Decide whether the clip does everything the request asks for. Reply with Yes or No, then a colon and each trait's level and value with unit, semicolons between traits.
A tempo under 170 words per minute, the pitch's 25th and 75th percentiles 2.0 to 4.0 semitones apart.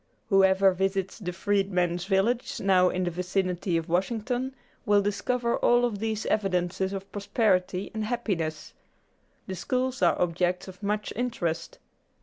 Yes: slow, 135 wpm; average, 3.0 semitones